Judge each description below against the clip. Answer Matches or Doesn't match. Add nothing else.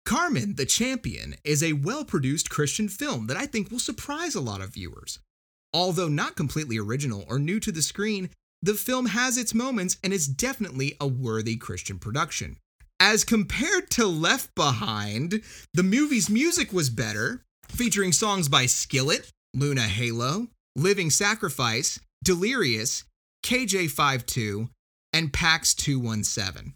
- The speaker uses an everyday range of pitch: Doesn't match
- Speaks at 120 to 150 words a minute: Matches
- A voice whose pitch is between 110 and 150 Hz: Doesn't match